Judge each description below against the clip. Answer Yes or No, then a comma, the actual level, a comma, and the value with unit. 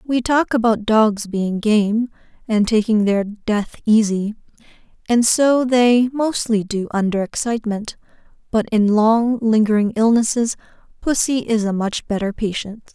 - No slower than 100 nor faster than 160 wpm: Yes, slow, 135 wpm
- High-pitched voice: Yes, high, 220 Hz